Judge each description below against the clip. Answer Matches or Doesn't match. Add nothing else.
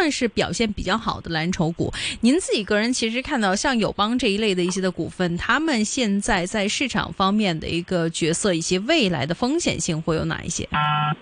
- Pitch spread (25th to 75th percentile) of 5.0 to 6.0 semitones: Matches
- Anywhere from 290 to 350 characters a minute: Matches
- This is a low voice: Doesn't match